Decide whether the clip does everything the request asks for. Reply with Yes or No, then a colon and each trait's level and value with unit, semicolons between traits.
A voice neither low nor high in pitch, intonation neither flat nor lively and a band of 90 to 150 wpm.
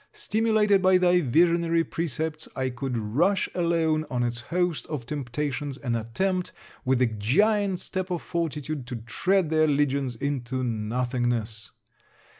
No: medium, 150 Hz; wide, 6.3 semitones; slow, 135 wpm